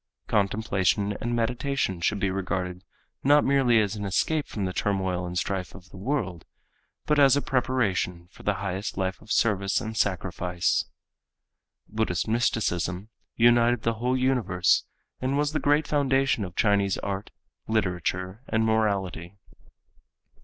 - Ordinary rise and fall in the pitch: Yes, average, 4.6 semitones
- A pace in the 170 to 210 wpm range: No, average, 140 wpm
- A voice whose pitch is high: No, low, 105 Hz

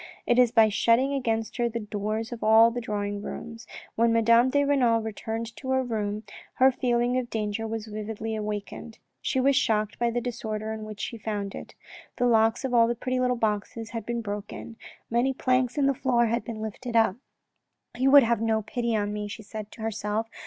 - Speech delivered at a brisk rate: Yes, fast, 210 wpm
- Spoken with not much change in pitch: Yes, narrow, 2.0 semitones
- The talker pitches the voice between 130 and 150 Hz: No, high, 225 Hz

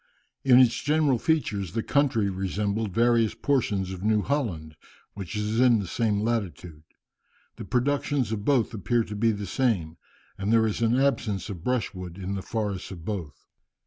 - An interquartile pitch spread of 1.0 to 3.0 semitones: No, average, 4.0 semitones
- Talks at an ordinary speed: Yes, average, 170 wpm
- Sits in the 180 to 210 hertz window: No, low, 110 Hz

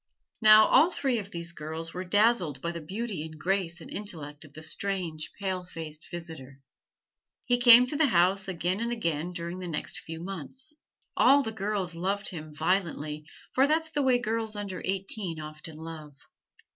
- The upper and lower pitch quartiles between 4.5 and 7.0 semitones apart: Yes, average, 5.2 semitones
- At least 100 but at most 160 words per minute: No, average, 175 wpm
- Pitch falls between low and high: Yes, medium, 180 Hz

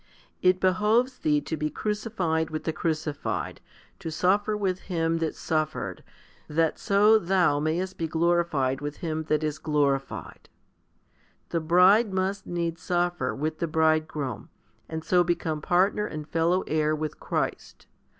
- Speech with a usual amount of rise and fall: Yes, average, 3.0 semitones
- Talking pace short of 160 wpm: Yes, average, 140 wpm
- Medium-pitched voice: Yes, medium, 165 Hz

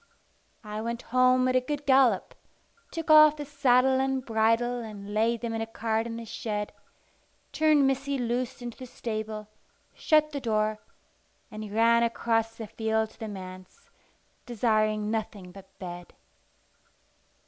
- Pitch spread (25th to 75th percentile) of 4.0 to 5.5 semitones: No, average, 3.0 semitones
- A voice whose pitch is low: No, high, 230 Hz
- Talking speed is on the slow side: No, average, 150 wpm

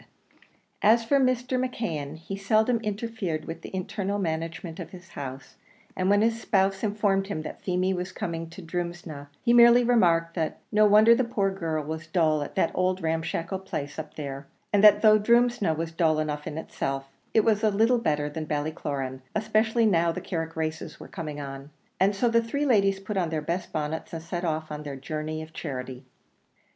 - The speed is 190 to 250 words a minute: Yes, average, 195 wpm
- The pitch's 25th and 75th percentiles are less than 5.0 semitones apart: No, average, 5.3 semitones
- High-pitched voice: No, medium, 175 Hz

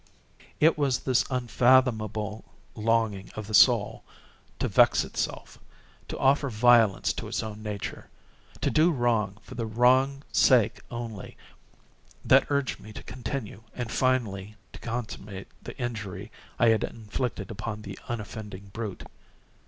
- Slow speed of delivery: Yes, slow, 125 wpm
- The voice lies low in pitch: Yes, low, 115 Hz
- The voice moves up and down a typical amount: Yes, average, 3.0 semitones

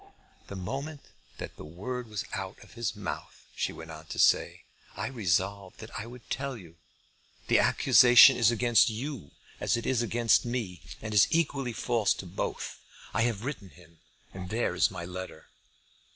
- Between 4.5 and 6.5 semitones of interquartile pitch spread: Yes, average, 4.8 semitones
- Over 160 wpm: Yes, average, 180 wpm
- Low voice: Yes, low, 110 Hz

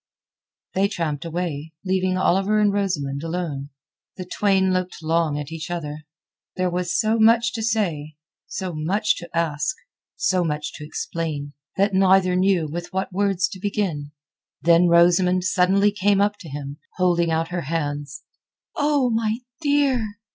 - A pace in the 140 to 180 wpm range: Yes, average, 155 wpm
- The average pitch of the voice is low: No, medium, 180 Hz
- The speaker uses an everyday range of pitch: Yes, average, 3.8 semitones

